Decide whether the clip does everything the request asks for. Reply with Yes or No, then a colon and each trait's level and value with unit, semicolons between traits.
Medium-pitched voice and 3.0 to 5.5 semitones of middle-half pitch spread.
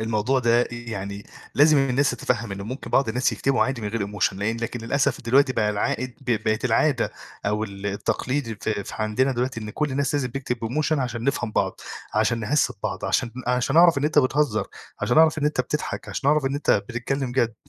No: low, 125 Hz; average, 3.7 semitones